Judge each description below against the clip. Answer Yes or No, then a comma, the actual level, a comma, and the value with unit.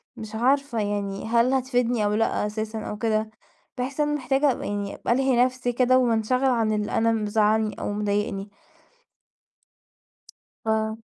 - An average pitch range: Yes, average, 3.2 semitones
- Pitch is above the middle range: Yes, high, 225 Hz